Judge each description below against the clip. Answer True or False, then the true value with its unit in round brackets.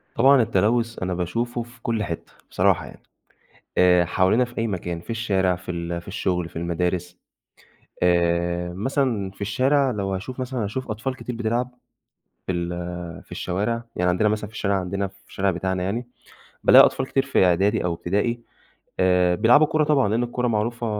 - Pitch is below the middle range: True (100 Hz)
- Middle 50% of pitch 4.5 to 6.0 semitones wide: True (4.9 semitones)